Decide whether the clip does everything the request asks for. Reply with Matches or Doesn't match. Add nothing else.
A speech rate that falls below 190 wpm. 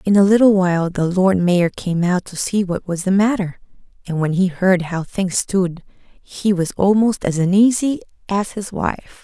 Doesn't match